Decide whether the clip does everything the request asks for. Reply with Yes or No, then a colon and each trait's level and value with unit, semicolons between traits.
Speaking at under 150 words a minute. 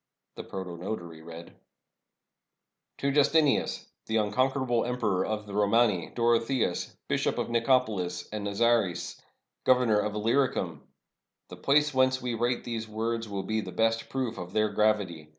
Yes: average, 140 wpm